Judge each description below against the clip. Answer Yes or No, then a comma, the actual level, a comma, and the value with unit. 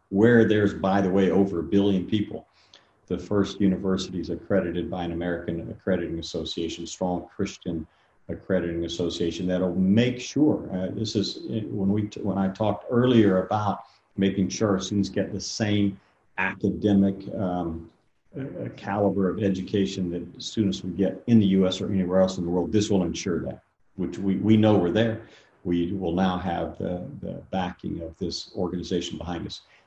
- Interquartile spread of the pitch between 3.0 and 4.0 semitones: No, narrow, 2.5 semitones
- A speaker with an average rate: Yes, average, 170 wpm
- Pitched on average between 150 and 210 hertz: No, very low, 95 Hz